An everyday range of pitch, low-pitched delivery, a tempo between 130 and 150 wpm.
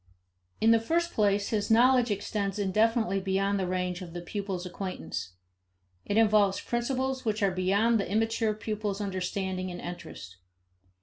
No: average, 3.1 semitones; high, 205 Hz; average, 145 wpm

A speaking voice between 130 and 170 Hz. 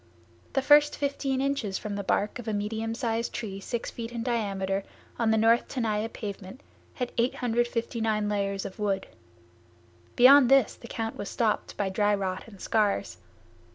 No: high, 225 Hz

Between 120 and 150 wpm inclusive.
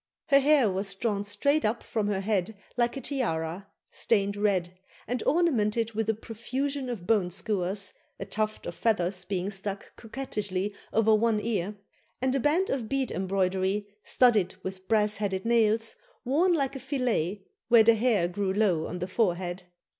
No: average, 165 wpm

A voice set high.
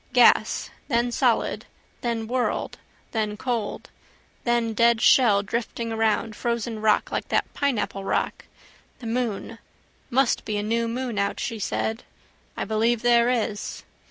Yes: high, 230 Hz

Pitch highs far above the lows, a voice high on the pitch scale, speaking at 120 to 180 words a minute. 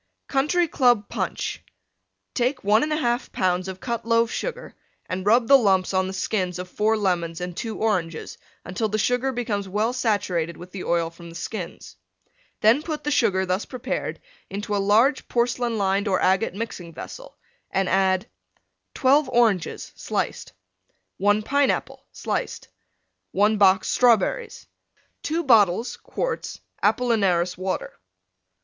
No: average, 4.7 semitones; high, 210 Hz; average, 140 wpm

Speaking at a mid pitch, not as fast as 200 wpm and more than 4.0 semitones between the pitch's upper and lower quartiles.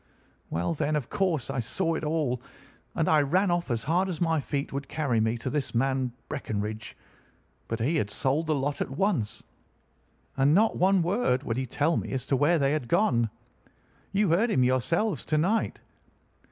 Yes: medium, 145 Hz; average, 190 wpm; average, 5.0 semitones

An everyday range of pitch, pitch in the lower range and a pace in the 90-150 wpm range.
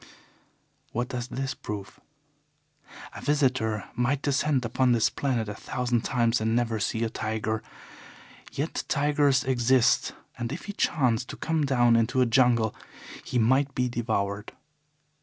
Yes: average, 3.0 semitones; low, 120 Hz; average, 140 wpm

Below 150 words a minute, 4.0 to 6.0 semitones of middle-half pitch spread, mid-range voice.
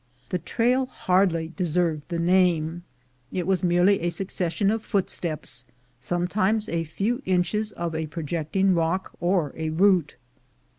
No: average, 140 wpm; average, 2.9 semitones; medium, 175 Hz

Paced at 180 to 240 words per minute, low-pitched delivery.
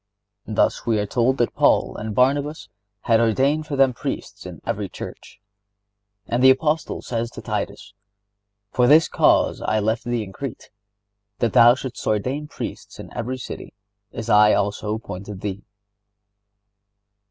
No: average, 150 wpm; low, 115 Hz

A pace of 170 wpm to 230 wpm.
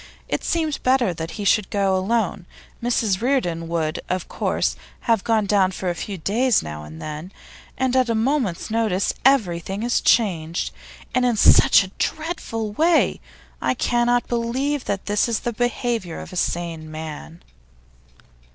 No: average, 160 wpm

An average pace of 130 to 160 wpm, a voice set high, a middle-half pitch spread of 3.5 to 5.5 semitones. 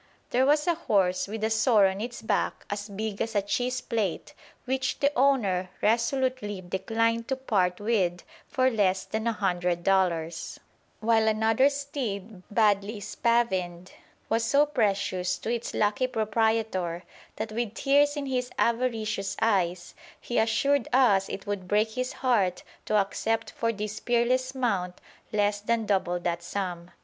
Yes: average, 150 wpm; high, 220 Hz; average, 3.8 semitones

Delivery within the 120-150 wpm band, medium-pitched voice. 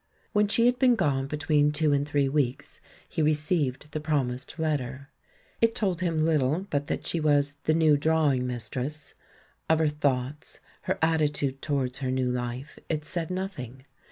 No: average, 165 wpm; medium, 150 Hz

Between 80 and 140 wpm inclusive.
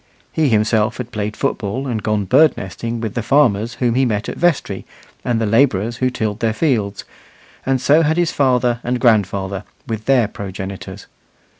No: average, 175 wpm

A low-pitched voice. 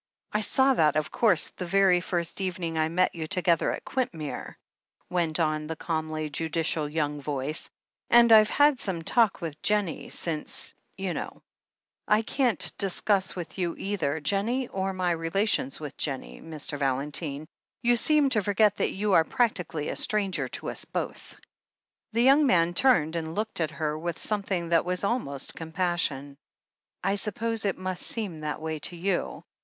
No: medium, 175 Hz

